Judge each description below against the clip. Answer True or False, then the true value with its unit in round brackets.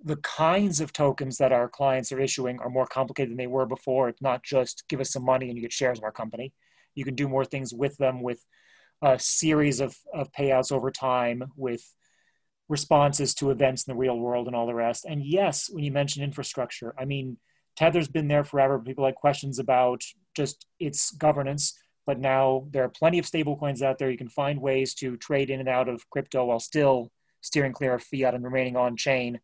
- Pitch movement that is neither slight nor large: False (2.0 semitones)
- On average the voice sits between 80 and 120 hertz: False (135 Hz)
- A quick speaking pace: True (220 wpm)